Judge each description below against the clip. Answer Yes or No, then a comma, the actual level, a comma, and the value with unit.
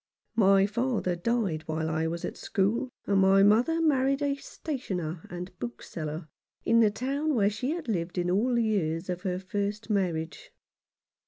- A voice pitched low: No, high, 200 Hz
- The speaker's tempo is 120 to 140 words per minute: No, average, 165 wpm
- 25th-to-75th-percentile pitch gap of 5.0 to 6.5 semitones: Yes, wide, 5.4 semitones